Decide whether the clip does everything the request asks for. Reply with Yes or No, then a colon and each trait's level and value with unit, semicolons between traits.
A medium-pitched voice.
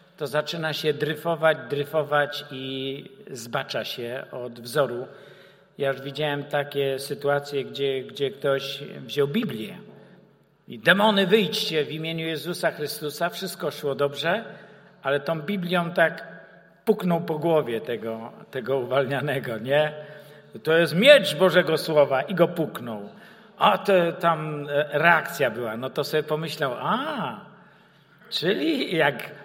Yes: medium, 150 Hz